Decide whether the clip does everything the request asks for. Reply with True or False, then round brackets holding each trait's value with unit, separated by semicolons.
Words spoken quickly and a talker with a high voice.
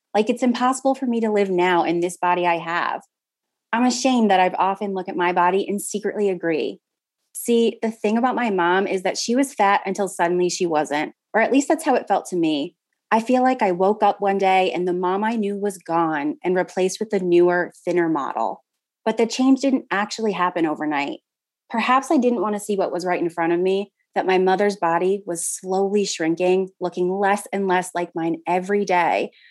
True (215 wpm; 195 Hz)